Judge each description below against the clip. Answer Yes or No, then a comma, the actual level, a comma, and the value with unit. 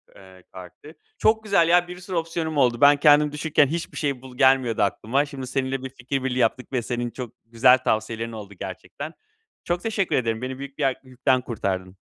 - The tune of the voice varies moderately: Yes, average, 4.2 semitones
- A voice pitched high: No, low, 130 Hz